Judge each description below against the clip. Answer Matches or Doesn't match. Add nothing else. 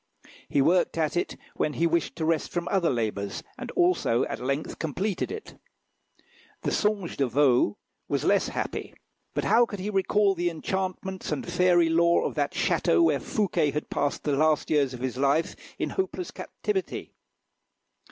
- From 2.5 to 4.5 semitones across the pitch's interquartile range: Doesn't match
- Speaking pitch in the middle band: Matches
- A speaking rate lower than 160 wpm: Doesn't match